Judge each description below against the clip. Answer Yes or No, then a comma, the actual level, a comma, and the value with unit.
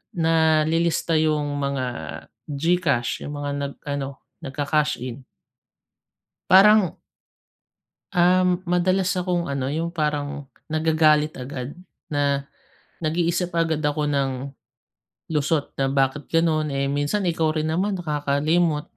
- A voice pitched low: No, medium, 155 Hz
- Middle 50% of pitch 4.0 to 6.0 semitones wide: No, average, 2.9 semitones